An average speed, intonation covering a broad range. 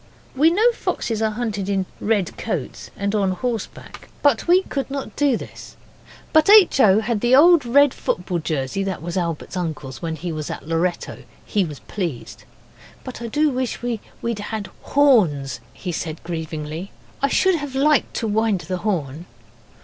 Yes: average, 170 wpm; wide, 7.2 semitones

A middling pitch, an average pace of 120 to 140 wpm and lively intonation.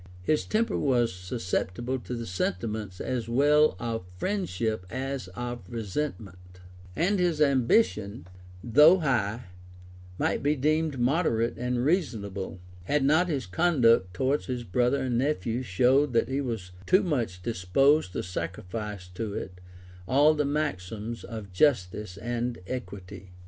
No: low, 120 Hz; slow, 135 wpm; wide, 6.1 semitones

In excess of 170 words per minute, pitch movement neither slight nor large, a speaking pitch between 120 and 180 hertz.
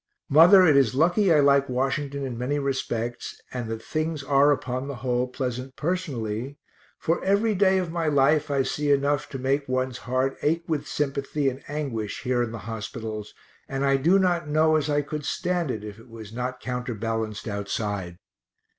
Yes: average, 180 wpm; average, 3.7 semitones; low, 135 Hz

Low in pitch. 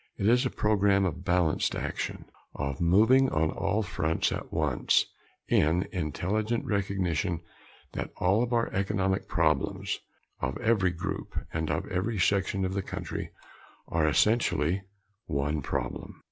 Yes: very low, 95 Hz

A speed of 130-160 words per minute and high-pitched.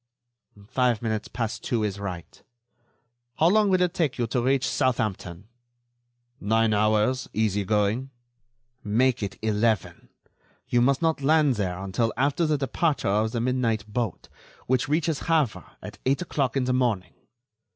No: average, 150 wpm; low, 120 Hz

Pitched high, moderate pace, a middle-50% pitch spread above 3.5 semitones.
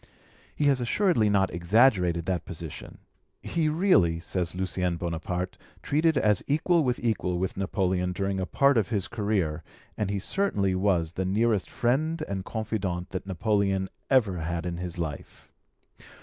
No: very low, 95 Hz; average, 150 wpm; average, 4.8 semitones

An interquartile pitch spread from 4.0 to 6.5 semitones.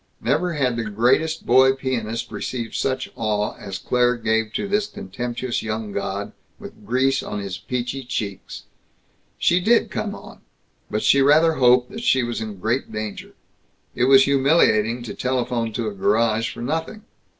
No: average, 3.6 semitones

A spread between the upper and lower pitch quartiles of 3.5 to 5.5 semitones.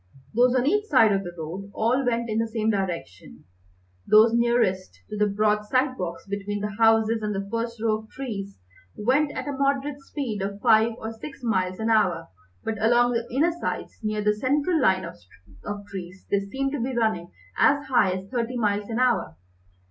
Yes: average, 3.8 semitones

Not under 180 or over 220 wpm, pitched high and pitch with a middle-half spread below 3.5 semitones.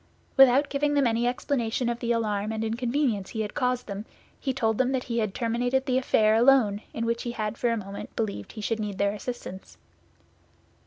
Yes: fast, 205 wpm; high, 230 Hz; average, 2.9 semitones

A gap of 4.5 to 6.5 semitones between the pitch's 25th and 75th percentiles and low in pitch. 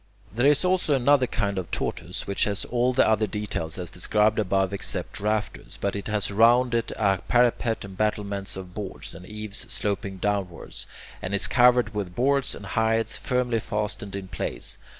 No: average, 3.4 semitones; low, 105 Hz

